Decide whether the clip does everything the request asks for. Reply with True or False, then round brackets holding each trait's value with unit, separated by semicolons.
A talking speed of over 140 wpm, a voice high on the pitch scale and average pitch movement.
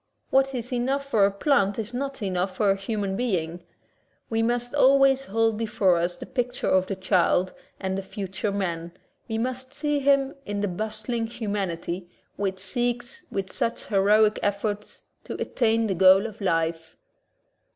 True (160 wpm; 210 Hz; 4.2 semitones)